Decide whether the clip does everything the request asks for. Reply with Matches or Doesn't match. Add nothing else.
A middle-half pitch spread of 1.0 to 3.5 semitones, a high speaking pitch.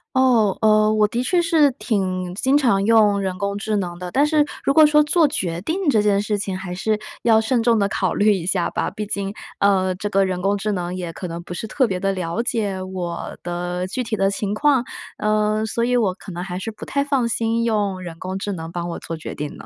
Doesn't match